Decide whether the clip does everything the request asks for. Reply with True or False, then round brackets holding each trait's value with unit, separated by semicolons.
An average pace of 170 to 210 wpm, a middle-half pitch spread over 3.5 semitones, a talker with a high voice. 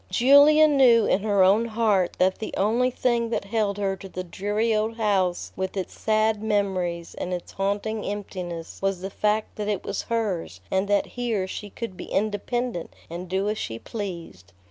False (185 wpm; 2.9 semitones; 205 Hz)